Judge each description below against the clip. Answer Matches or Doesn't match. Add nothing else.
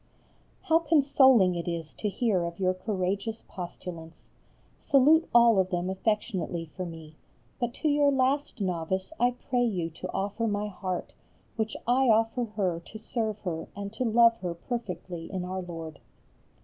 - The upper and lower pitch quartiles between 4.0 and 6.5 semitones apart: Matches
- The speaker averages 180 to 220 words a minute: Doesn't match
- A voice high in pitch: Matches